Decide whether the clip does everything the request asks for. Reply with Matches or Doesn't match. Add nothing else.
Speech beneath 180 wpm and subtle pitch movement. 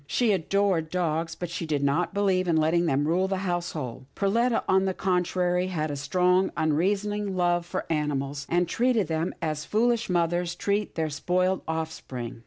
Doesn't match